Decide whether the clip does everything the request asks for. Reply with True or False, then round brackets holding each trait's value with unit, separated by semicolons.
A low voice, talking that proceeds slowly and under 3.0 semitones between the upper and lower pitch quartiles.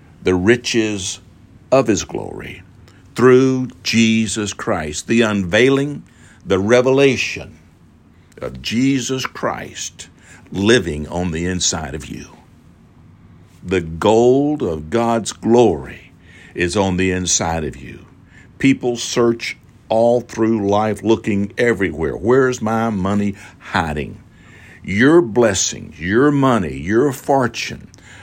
False (110 Hz; 105 wpm; 5.0 semitones)